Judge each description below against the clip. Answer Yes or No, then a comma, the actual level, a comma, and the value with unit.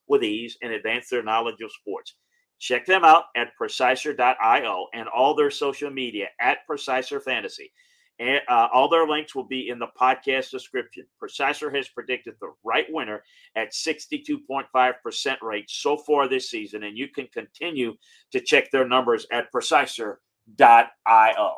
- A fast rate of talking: No, average, 155 wpm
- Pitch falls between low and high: Yes, medium, 150 Hz